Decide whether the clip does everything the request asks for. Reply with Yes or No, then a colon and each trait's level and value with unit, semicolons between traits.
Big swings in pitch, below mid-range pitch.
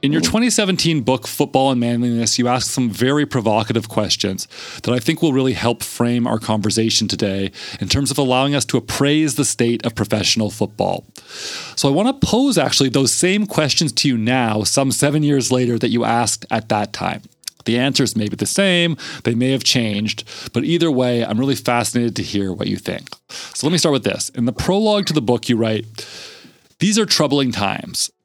No: average, 4.3 semitones; low, 125 Hz